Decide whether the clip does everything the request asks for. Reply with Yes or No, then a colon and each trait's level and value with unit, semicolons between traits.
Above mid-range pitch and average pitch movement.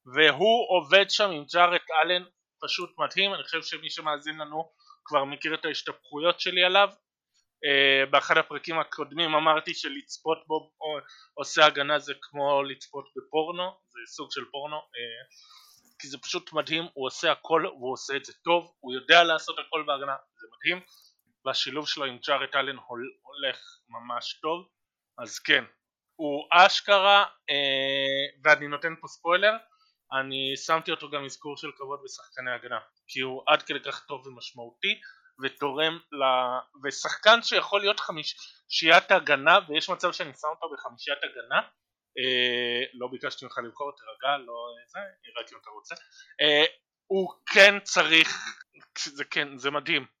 No: medium, 155 Hz; average, 4.3 semitones